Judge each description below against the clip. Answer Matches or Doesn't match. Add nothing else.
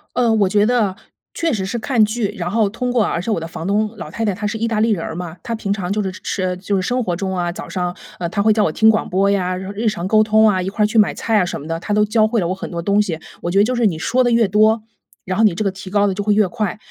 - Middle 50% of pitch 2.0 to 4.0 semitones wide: Matches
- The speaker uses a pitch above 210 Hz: Doesn't match